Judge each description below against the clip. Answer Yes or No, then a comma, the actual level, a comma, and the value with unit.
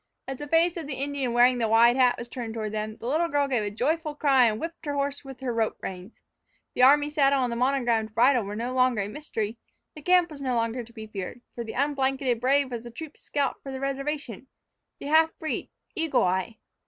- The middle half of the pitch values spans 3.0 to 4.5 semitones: Yes, average, 3.7 semitones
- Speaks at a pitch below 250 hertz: No, very high, 255 Hz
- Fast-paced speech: Yes, fast, 230 wpm